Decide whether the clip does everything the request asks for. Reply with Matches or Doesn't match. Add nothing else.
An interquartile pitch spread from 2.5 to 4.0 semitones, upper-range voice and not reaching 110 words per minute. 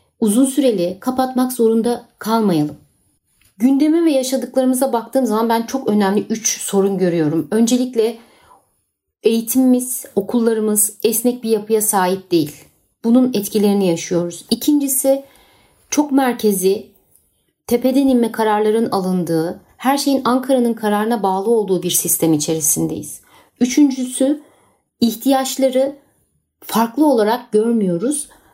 Doesn't match